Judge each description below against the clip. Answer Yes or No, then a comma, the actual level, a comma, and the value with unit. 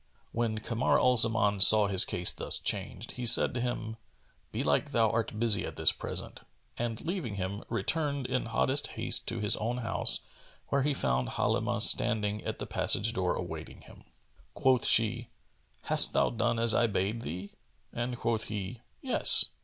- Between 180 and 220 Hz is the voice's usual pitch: No, low, 115 Hz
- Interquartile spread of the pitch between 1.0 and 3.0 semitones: Yes, narrow, 2.6 semitones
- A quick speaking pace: No, average, 170 wpm